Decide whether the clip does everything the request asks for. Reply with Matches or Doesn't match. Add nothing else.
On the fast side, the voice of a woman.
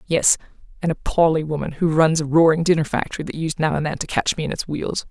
Matches